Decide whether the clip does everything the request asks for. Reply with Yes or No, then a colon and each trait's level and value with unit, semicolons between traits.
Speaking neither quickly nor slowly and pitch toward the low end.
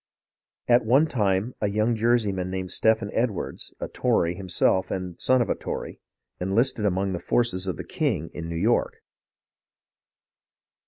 Yes: average, 160 wpm; low, 100 Hz